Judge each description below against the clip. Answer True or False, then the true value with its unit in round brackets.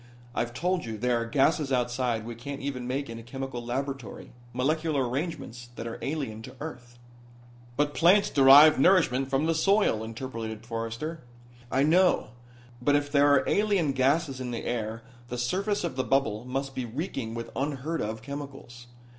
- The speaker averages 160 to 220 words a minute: True (170 wpm)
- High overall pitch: False (135 Hz)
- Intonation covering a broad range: False (3.6 semitones)